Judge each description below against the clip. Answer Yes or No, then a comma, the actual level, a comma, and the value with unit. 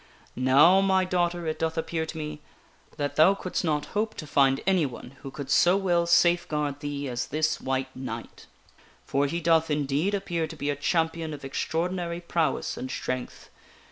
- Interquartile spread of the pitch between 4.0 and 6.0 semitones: No, average, 3.5 semitones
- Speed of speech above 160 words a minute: Yes, average, 170 wpm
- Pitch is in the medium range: Yes, medium, 155 Hz